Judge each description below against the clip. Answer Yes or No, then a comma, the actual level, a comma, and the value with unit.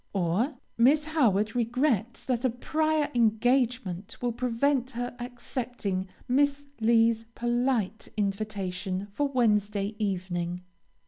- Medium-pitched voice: No, high, 235 Hz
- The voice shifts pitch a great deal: No, average, 3.9 semitones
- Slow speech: Yes, slow, 105 wpm